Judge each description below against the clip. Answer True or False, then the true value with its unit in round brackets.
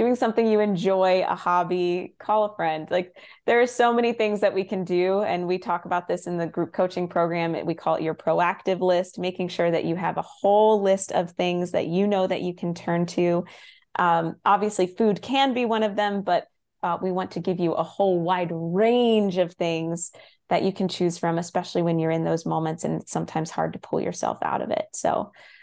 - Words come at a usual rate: False (225 wpm)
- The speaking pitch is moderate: True (180 Hz)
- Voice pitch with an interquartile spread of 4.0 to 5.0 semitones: False (2.8 semitones)